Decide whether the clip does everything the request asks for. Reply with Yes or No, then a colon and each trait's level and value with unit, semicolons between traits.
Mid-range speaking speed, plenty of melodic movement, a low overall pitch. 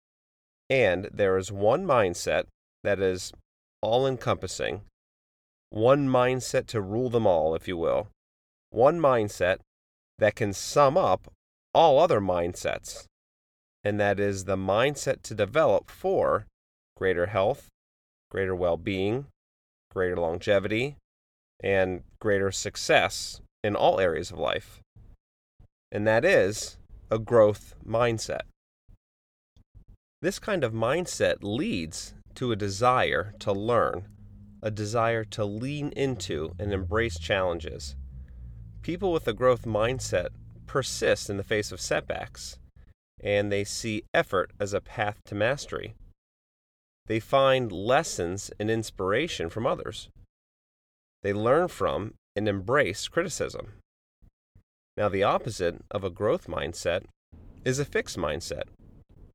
No: slow, 120 wpm; wide, 7.4 semitones; low, 100 Hz